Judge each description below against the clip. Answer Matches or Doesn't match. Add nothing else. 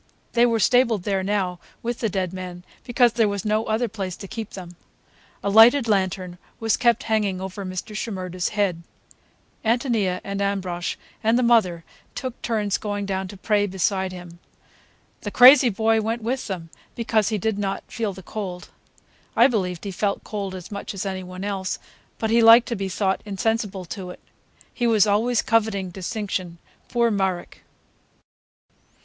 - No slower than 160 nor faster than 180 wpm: Matches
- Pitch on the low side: Doesn't match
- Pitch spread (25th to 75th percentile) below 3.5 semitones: Matches